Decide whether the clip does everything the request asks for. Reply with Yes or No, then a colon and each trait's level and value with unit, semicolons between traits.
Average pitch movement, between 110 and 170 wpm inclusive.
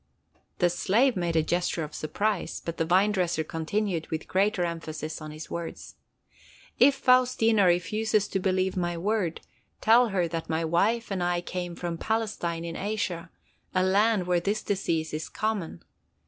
Yes: average, 4.1 semitones; average, 160 wpm